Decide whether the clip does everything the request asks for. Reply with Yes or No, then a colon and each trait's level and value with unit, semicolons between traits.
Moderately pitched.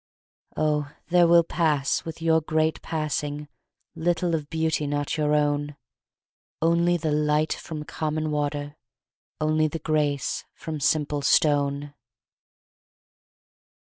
Yes: medium, 155 Hz